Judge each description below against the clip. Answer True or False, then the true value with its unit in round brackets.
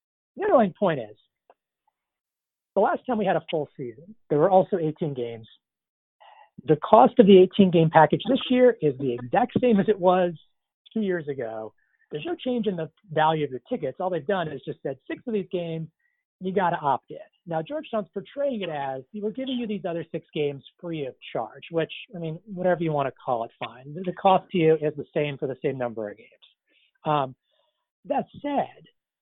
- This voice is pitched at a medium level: True (175 Hz)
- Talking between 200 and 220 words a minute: True (205 wpm)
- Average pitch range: False (6.4 semitones)